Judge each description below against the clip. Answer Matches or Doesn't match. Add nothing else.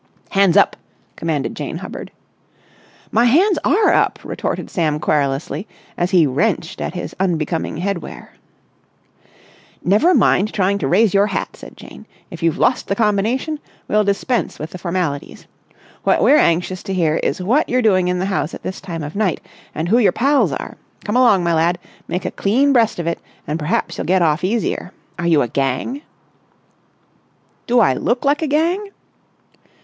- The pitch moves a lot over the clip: Matches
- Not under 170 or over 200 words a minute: Matches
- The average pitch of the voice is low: Doesn't match